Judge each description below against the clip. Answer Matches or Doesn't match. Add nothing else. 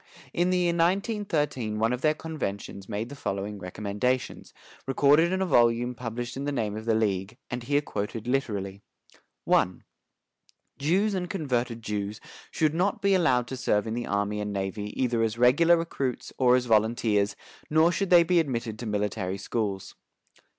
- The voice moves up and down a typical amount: Doesn't match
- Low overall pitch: Matches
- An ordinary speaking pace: Matches